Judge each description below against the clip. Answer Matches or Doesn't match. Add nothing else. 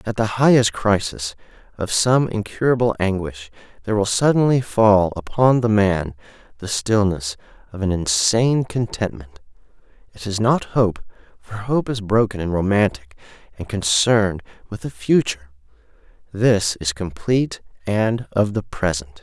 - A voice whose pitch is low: Matches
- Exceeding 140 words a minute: Doesn't match